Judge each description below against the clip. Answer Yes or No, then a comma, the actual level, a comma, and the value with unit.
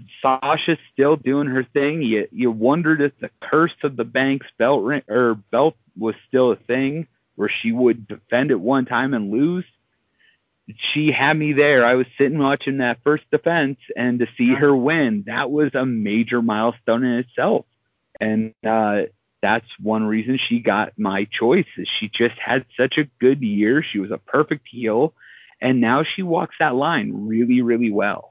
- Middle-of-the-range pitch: No, low, 125 Hz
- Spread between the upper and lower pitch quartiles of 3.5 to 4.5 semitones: Yes, average, 4.2 semitones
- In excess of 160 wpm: Yes, average, 175 wpm